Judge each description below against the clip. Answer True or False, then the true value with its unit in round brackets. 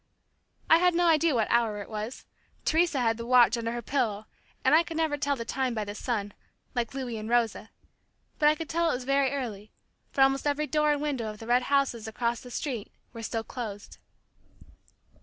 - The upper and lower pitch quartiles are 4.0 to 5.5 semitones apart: True (4.4 semitones)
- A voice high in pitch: True (250 Hz)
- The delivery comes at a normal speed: False (210 wpm)